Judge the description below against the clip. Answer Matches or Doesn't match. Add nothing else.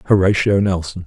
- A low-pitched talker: Matches